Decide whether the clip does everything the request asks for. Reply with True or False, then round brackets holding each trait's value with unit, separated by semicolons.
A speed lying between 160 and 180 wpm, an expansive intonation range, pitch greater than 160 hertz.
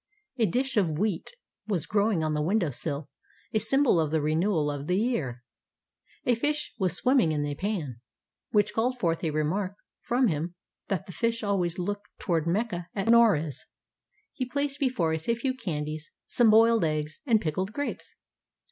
True (175 wpm; 6.6 semitones; 190 Hz)